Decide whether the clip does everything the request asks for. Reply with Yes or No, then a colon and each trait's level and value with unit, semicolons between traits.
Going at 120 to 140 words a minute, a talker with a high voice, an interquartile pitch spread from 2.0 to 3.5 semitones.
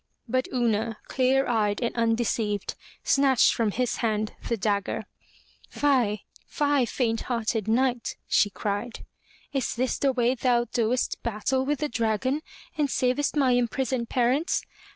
Yes: slow, 135 wpm; high, 240 Hz; average, 2.8 semitones